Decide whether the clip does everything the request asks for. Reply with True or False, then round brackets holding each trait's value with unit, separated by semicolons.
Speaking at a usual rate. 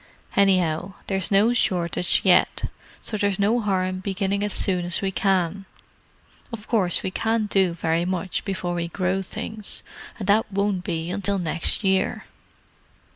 True (150 wpm)